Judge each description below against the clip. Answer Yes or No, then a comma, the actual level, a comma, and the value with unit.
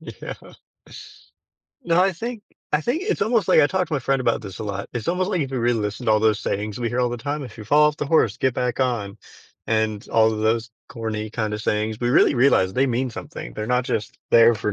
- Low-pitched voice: Yes, low, 120 Hz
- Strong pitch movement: No, average, 4.9 semitones